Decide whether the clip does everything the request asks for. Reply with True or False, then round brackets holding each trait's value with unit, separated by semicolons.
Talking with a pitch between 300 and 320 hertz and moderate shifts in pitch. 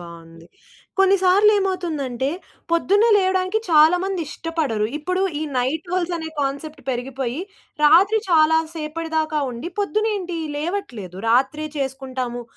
False (315 Hz; 5.8 semitones)